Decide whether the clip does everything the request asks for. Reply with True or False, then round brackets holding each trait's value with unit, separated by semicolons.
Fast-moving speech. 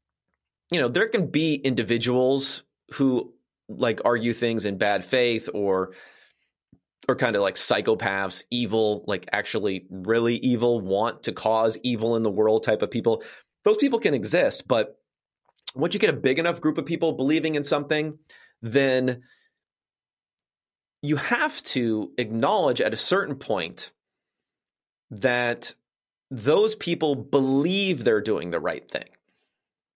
False (140 wpm)